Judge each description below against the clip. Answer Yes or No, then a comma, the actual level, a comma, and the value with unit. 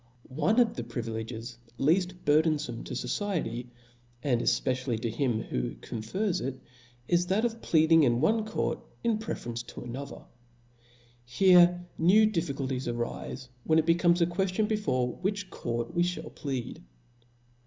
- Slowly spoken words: No, average, 145 wpm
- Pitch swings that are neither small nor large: No, wide, 6.9 semitones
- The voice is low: No, medium, 155 Hz